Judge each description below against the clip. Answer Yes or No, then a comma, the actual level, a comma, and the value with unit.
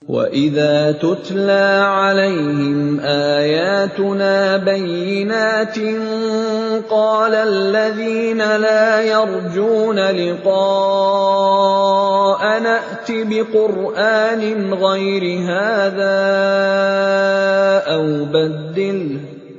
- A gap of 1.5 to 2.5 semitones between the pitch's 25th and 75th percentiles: Yes, narrow, 2.1 semitones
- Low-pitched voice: No, high, 195 Hz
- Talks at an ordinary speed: No, slow, 50 wpm